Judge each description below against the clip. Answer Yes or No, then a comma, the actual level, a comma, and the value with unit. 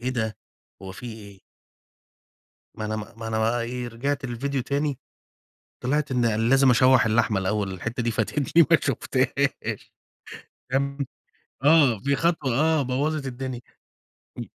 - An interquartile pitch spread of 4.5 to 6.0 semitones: No, average, 3.7 semitones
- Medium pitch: No, low, 125 Hz